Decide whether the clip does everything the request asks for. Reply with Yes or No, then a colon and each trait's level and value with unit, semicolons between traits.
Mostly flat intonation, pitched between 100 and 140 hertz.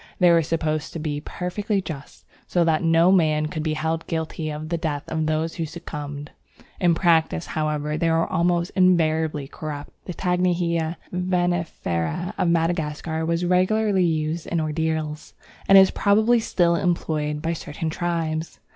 No: narrow, 2.2 semitones; medium, 165 Hz